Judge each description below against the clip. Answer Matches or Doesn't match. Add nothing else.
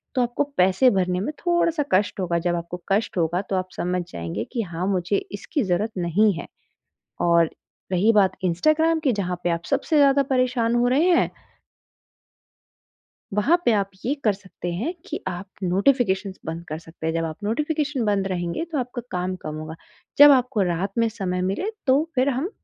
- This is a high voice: Matches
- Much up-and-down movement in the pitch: Matches